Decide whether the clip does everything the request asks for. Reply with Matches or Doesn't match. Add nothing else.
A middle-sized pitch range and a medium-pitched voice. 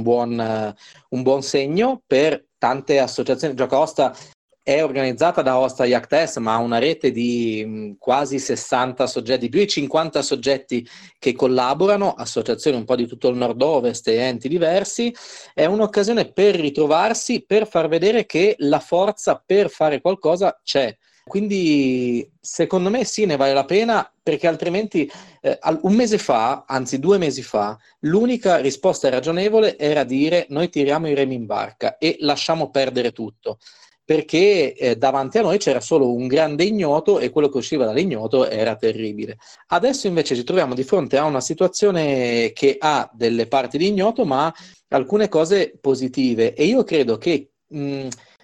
Doesn't match